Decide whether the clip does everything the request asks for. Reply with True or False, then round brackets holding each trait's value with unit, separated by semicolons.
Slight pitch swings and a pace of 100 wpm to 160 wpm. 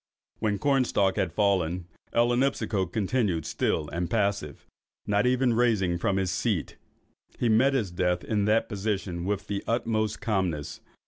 False (3.9 semitones; 140 wpm)